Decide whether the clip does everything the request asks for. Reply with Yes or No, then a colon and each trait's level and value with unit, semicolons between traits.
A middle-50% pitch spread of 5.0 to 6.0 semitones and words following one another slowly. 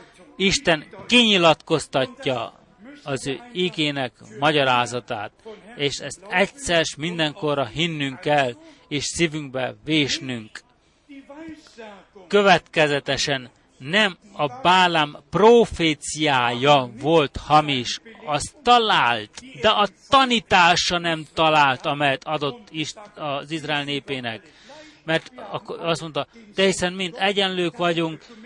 Yes: wide, 5.5 semitones; slow, 90 wpm